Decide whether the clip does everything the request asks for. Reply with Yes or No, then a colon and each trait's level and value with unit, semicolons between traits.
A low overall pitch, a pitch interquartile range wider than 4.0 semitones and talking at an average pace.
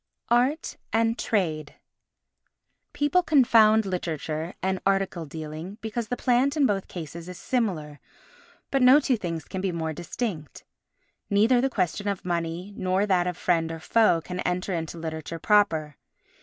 No: medium, 185 Hz; wide, 5.4 semitones; average, 150 wpm